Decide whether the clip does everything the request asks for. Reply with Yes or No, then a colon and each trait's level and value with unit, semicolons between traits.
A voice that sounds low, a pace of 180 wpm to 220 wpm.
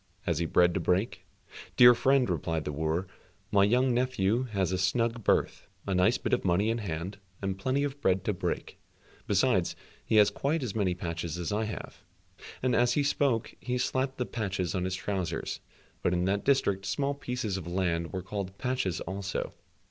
Yes: low, 100 Hz; average, 190 wpm